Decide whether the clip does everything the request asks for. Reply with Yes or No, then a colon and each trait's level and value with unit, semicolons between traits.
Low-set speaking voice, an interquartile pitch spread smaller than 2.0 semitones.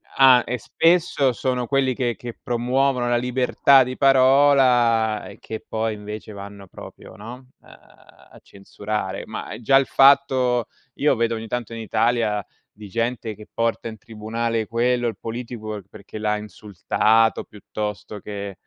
No: low, 115 Hz; average, 2.8 semitones